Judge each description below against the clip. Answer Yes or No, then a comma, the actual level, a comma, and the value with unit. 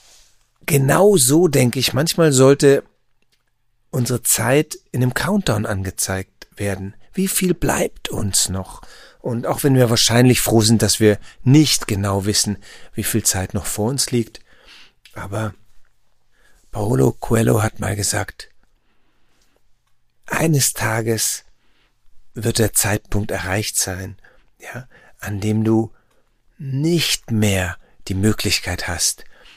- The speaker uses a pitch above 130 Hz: No, low, 110 Hz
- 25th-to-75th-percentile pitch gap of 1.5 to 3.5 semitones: No, average, 4.2 semitones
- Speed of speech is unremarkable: No, slow, 120 wpm